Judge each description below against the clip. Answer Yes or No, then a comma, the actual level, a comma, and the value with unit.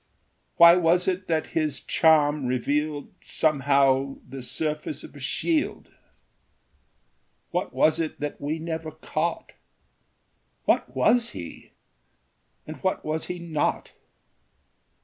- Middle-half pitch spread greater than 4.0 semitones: No, average, 2.8 semitones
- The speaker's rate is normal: No, slow, 110 wpm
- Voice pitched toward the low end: No, medium, 155 Hz